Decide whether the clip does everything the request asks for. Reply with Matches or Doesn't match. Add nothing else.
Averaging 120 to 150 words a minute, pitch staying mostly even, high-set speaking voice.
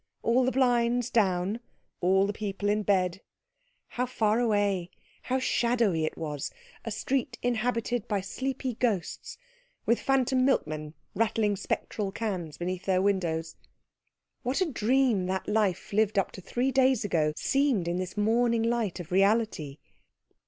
Doesn't match